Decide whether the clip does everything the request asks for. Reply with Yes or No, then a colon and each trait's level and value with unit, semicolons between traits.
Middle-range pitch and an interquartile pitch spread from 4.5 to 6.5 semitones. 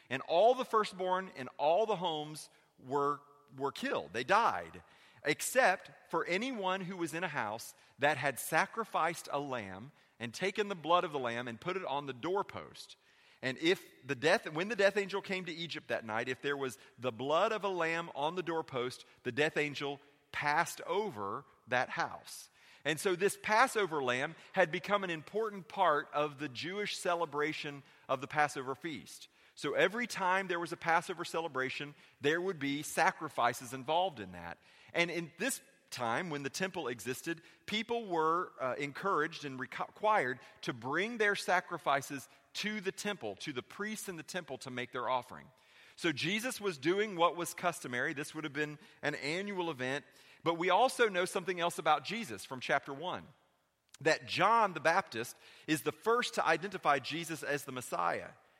Yes: medium, 165 Hz; average, 5.0 semitones